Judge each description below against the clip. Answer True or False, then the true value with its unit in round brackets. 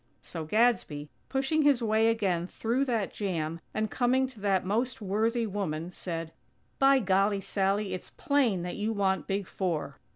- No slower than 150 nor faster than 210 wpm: True (160 wpm)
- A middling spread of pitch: True (4.2 semitones)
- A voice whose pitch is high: True (205 Hz)